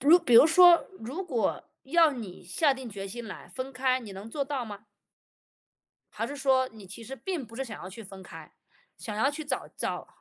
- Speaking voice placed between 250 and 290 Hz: Yes, very high, 255 Hz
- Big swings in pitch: No, average, 4.8 semitones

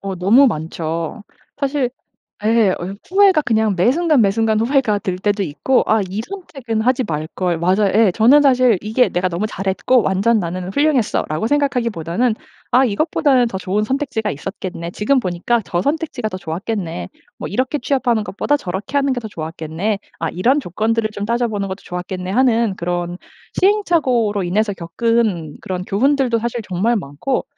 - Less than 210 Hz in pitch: No, high, 215 Hz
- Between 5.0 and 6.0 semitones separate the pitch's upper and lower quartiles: Yes, wide, 5.5 semitones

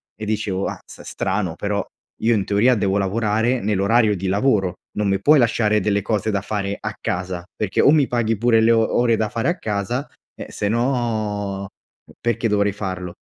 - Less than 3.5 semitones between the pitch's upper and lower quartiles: Yes, average, 2.7 semitones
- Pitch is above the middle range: No, low, 105 Hz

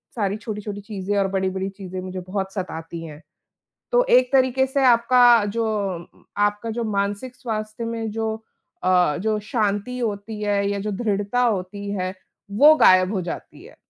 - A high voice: Yes, high, 205 Hz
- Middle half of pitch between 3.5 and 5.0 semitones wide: No, average, 2.9 semitones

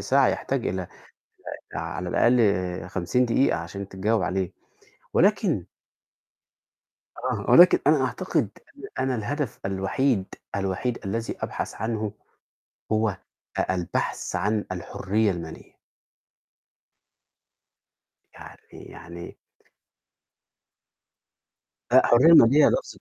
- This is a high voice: No, low, 105 Hz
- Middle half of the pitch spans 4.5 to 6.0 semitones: Yes, average, 5.0 semitones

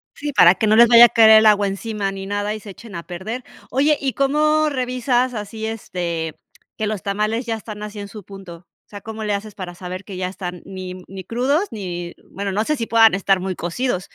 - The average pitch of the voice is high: Yes, high, 210 Hz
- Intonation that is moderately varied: Yes, average, 3.4 semitones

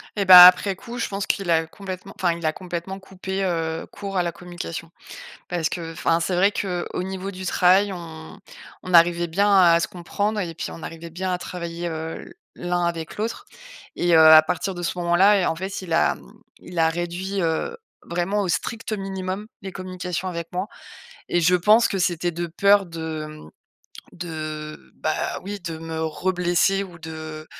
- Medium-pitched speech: Yes, medium, 175 Hz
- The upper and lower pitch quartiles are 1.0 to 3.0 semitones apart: Yes, narrow, 2.4 semitones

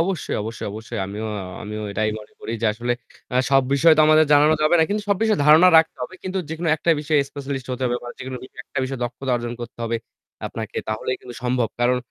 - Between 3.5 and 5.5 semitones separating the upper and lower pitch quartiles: Yes, average, 5.0 semitones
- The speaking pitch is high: No, low, 130 Hz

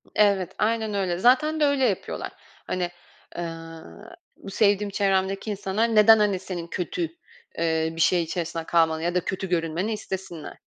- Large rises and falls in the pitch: No, average, 3.8 semitones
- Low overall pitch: No, high, 190 Hz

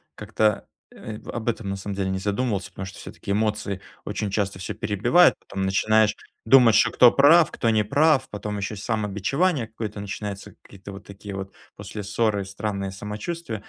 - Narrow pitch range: Yes, narrow, 2.3 semitones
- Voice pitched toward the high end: No, low, 105 Hz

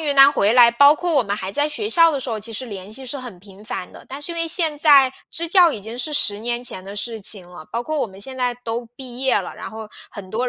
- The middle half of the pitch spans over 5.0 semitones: Yes, wide, 5.5 semitones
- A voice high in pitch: Yes, high, 245 Hz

